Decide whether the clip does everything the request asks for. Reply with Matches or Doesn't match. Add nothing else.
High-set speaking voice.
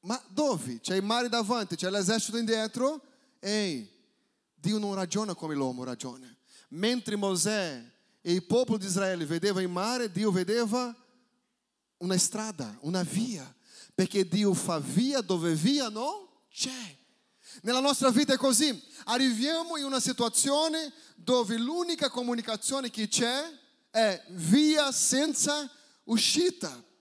Matches